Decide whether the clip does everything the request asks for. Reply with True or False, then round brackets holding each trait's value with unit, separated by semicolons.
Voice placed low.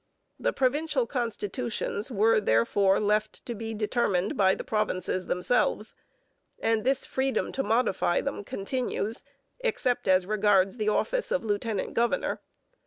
False (215 Hz)